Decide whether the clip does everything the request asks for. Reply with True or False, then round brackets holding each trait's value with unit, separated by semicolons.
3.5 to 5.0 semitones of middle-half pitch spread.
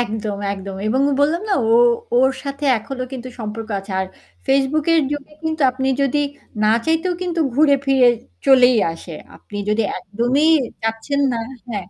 True (4.7 semitones)